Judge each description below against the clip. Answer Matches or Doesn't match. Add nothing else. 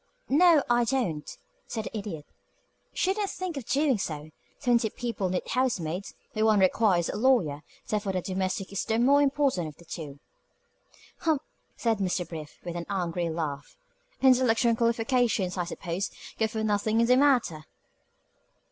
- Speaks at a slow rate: Doesn't match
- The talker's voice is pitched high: Matches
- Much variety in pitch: Matches